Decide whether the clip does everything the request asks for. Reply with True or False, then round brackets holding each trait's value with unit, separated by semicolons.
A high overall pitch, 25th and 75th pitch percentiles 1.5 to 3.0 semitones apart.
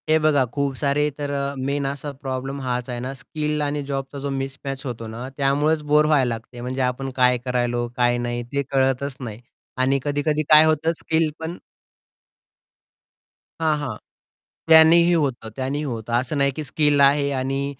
False (140 Hz; 2.6 semitones)